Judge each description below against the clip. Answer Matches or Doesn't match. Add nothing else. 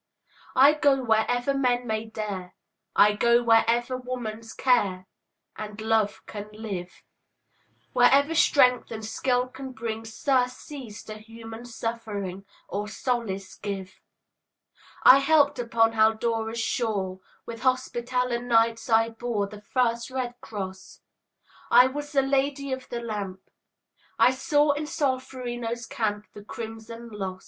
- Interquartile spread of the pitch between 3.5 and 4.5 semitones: Doesn't match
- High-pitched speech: Matches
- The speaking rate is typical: Doesn't match